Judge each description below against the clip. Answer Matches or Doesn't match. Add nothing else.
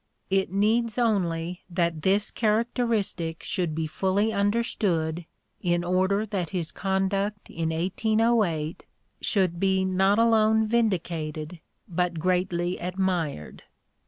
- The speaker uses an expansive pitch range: Doesn't match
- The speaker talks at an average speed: Doesn't match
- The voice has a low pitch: Doesn't match